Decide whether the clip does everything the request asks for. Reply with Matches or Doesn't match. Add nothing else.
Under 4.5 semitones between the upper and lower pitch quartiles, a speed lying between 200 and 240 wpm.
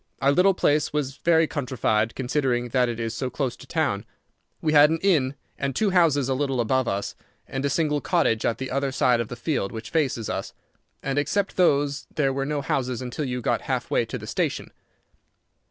Matches